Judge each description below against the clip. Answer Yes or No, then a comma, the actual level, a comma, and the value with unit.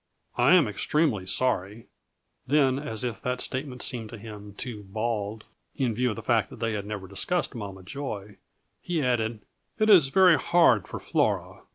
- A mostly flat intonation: No, average, 4.4 semitones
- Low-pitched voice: Yes, low, 115 Hz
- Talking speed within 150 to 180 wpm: Yes, average, 175 wpm